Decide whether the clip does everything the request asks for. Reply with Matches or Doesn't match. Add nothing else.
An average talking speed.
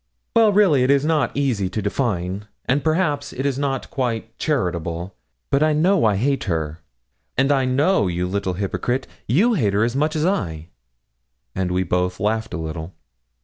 Matches